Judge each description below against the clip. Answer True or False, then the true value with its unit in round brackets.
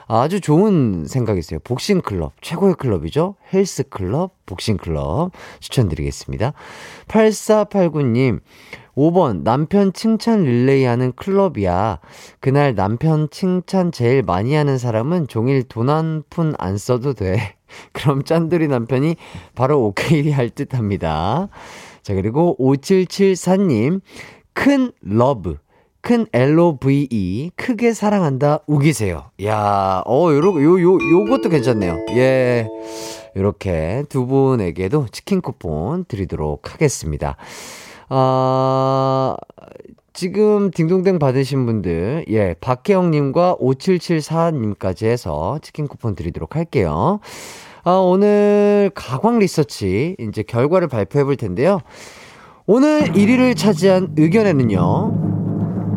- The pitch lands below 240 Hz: True (140 Hz)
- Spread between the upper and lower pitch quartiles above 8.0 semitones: True (8.6 semitones)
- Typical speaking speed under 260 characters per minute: True (235 characters per minute)